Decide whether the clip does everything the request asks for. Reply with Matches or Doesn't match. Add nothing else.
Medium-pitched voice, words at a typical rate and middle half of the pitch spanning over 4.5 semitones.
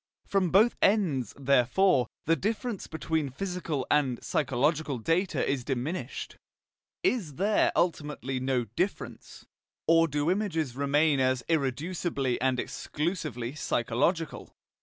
Doesn't match